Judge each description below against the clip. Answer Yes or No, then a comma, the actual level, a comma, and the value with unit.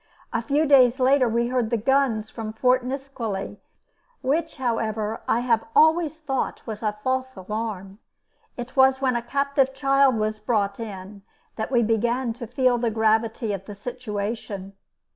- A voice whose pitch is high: Yes, high, 235 Hz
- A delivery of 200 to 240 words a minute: No, average, 160 wpm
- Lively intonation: No, average, 3.4 semitones